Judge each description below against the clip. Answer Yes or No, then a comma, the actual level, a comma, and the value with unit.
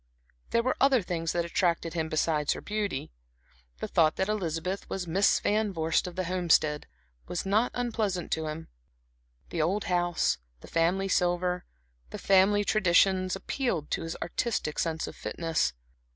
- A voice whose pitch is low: No, medium, 180 Hz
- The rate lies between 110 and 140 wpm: No, average, 155 wpm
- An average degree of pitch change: Yes, average, 3.3 semitones